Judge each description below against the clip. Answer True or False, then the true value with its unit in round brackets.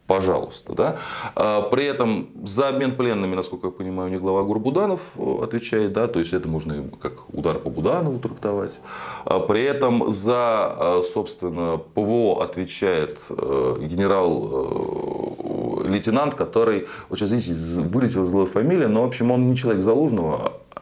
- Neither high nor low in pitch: False (115 Hz)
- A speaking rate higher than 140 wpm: False (135 wpm)